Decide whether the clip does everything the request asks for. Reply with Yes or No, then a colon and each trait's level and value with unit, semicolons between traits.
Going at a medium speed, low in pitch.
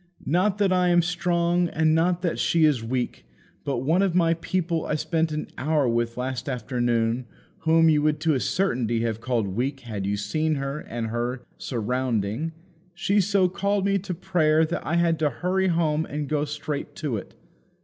No: average, 190 wpm; medium, 155 Hz